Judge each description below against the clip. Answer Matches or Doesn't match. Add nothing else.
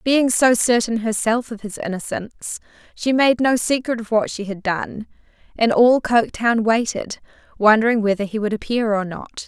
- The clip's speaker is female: Matches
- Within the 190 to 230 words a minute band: Doesn't match